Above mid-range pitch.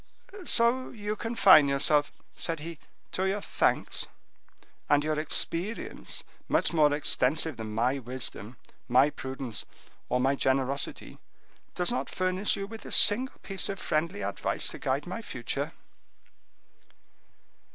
No: medium, 155 Hz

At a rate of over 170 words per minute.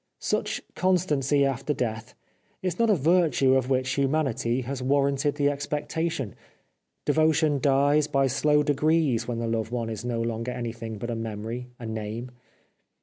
No: average, 150 wpm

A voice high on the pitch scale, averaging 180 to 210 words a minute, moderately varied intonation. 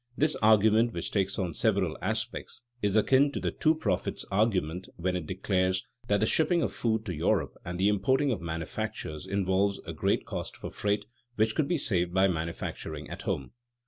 No: low, 100 Hz; average, 185 wpm; average, 3.5 semitones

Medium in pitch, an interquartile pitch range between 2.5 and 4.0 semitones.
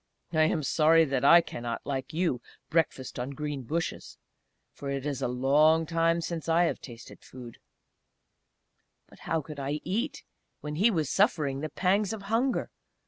Yes: medium, 155 Hz; average, 3.7 semitones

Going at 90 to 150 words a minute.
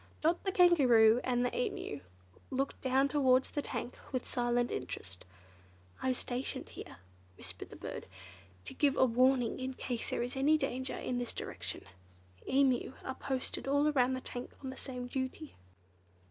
No: average, 160 wpm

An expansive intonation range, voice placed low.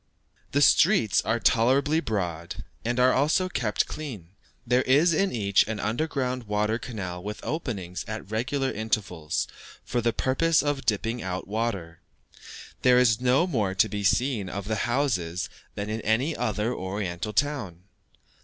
No: average, 4.7 semitones; low, 115 Hz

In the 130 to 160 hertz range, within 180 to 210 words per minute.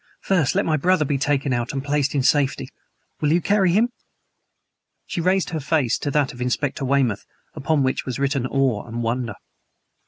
Yes: medium, 140 Hz; average, 185 wpm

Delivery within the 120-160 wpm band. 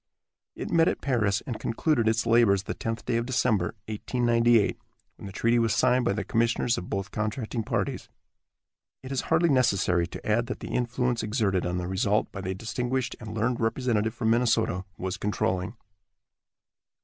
No: average, 175 wpm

